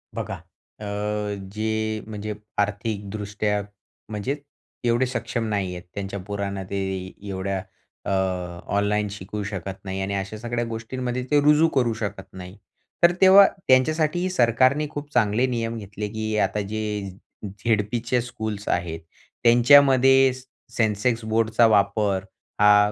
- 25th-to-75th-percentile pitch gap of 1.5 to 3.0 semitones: No, average, 3.4 semitones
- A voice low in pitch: Yes, low, 110 Hz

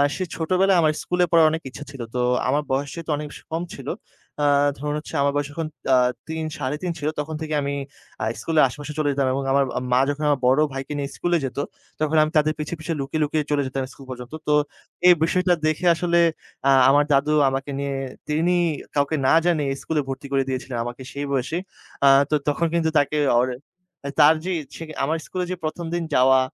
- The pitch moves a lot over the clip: No, average, 2.8 semitones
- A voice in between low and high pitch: Yes, medium, 150 Hz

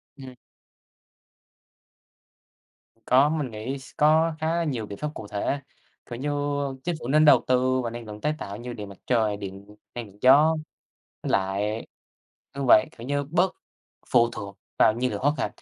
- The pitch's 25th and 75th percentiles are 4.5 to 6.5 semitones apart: Yes, wide, 5.6 semitones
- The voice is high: No, low, 125 Hz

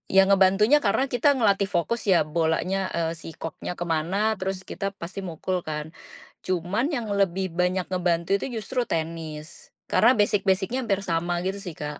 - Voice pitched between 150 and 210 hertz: Yes, medium, 185 Hz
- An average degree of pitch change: Yes, average, 3.0 semitones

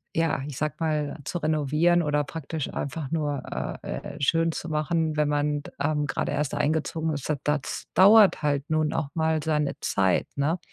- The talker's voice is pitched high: No, medium, 150 Hz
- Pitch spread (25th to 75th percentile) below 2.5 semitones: Yes, narrow, 1.8 semitones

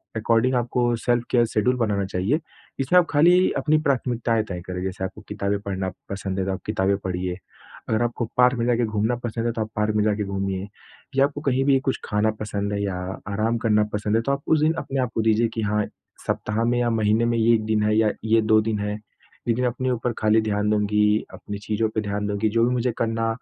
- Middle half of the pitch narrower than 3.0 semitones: Yes, narrow, 2.6 semitones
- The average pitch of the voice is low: Yes, low, 110 Hz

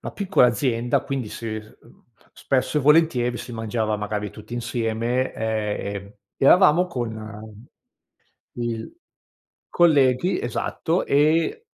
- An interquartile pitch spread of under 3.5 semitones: No, average, 5.0 semitones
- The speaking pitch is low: Yes, low, 120 Hz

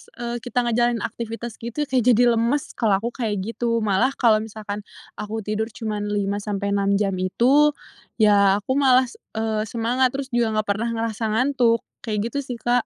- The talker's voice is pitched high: Yes, high, 230 Hz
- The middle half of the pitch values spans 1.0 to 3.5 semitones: Yes, narrow, 2.4 semitones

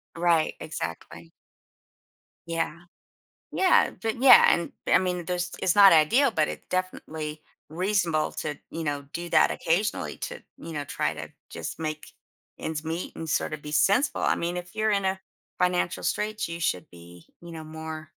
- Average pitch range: Yes, average, 3.1 semitones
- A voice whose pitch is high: No, medium, 165 Hz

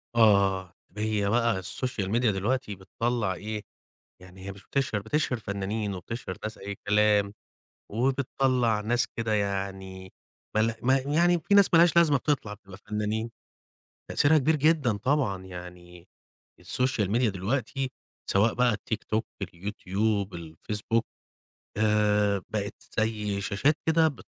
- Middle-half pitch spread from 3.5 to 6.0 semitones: Yes, average, 4.1 semitones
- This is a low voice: Yes, low, 105 Hz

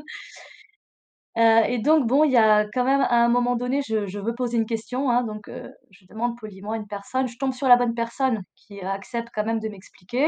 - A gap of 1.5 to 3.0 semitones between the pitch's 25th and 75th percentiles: Yes, average, 2.7 semitones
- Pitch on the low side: No, high, 230 Hz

